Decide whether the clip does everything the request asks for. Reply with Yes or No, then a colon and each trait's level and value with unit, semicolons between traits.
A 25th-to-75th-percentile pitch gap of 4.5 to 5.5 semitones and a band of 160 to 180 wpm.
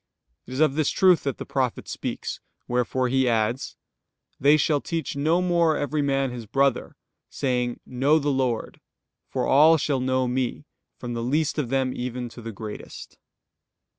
No: average, 3.0 semitones; average, 165 wpm